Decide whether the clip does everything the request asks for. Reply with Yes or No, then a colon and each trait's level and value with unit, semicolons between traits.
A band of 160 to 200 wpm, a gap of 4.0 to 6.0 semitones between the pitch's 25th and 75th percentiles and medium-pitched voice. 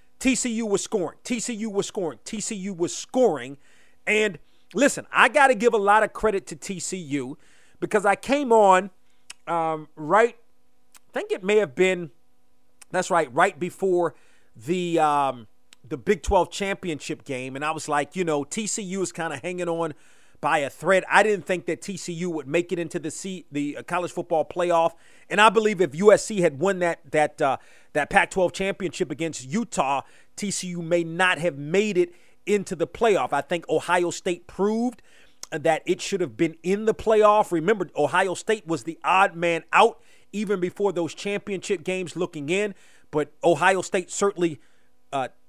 No: average, 175 wpm; average, 3.6 semitones; medium, 180 Hz